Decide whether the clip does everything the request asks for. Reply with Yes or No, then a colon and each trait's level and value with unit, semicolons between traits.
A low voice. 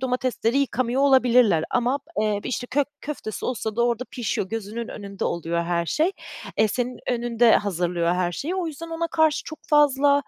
No: high, 245 Hz